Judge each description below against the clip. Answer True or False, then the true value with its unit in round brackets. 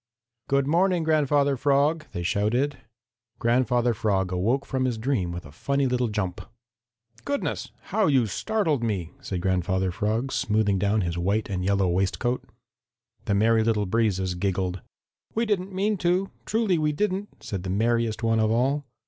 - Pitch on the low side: True (115 Hz)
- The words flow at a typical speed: True (155 wpm)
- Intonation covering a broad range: True (6.7 semitones)